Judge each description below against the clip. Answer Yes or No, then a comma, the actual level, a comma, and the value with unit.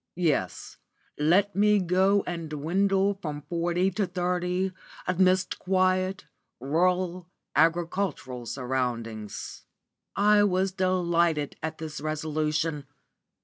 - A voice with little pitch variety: No, average, 3.4 semitones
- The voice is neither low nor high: Yes, medium, 175 Hz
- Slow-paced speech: Yes, slow, 95 wpm